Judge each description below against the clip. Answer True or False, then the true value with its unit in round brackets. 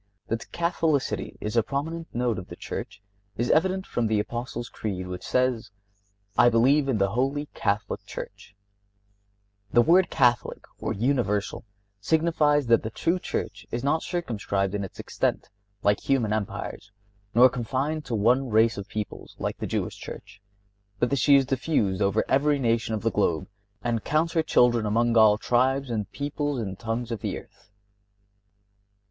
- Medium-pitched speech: False (120 Hz)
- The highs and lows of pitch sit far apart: False (4.7 semitones)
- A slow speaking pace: False (165 wpm)